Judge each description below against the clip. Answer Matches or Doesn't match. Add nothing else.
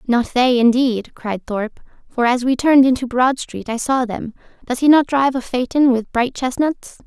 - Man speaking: Doesn't match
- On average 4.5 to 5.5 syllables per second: Matches